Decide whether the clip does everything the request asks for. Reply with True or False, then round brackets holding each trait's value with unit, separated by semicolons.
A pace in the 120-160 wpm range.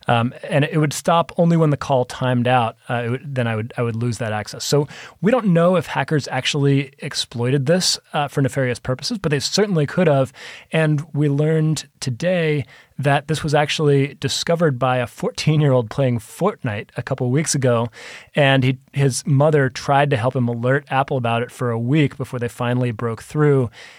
False (200 wpm)